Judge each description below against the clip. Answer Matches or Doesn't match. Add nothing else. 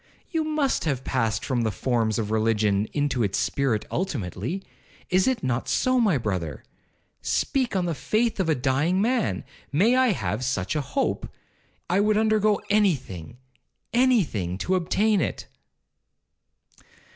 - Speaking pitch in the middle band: Matches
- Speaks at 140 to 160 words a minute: Matches